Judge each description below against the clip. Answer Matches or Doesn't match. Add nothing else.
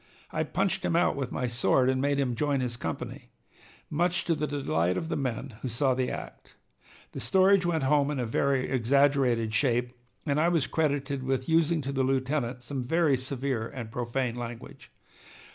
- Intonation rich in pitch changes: Doesn't match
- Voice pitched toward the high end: Doesn't match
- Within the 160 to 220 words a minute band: Matches